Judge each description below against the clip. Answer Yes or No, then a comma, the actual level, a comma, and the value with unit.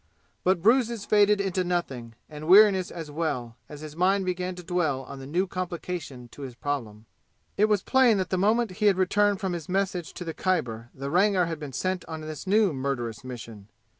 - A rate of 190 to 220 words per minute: Yes, average, 200 wpm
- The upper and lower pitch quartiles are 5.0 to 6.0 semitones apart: Yes, wide, 5.6 semitones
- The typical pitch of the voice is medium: Yes, medium, 175 Hz